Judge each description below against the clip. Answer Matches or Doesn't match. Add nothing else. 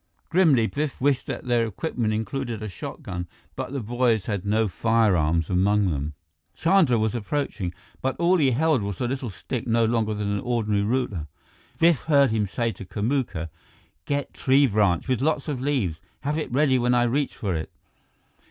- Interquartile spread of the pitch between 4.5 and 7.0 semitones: Matches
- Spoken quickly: Doesn't match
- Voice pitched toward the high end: Doesn't match